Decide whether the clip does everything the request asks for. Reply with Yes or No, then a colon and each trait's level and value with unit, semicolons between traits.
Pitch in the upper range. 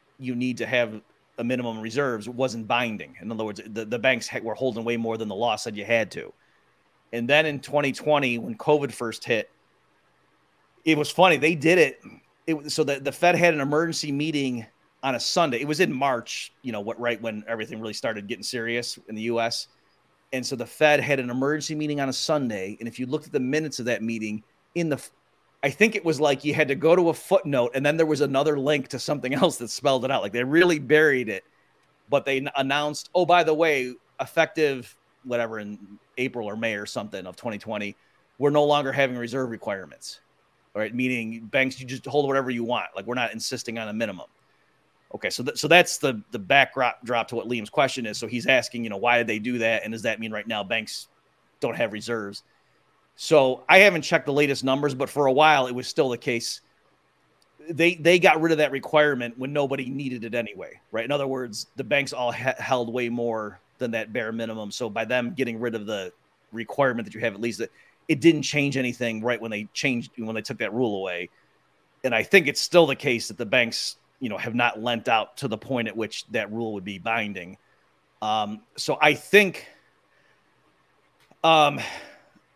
No: low, 130 Hz